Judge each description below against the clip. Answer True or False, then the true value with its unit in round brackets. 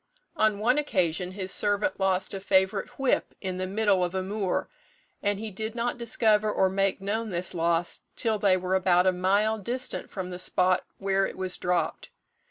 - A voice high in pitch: True (195 Hz)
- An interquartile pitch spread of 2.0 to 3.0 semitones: True (2.6 semitones)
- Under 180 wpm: False (185 wpm)